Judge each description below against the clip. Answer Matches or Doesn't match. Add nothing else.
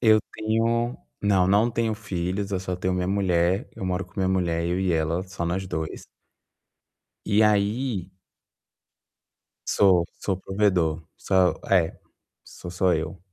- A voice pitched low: Matches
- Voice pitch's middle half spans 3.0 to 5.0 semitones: Doesn't match